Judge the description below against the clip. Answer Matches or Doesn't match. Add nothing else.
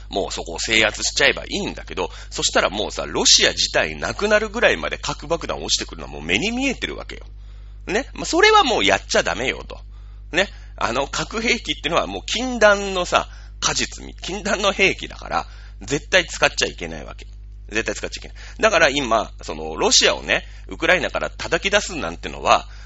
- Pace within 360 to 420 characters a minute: Matches